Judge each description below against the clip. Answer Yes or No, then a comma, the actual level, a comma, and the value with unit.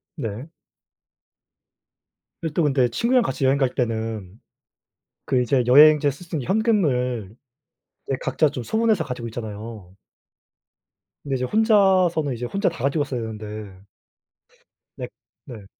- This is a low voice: Yes, low, 130 Hz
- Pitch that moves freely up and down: Yes, wide, 5.9 semitones